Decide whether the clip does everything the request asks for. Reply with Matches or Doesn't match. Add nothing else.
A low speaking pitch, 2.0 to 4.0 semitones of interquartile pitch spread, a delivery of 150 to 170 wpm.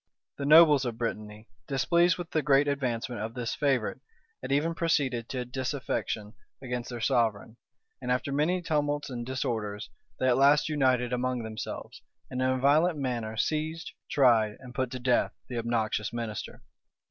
Matches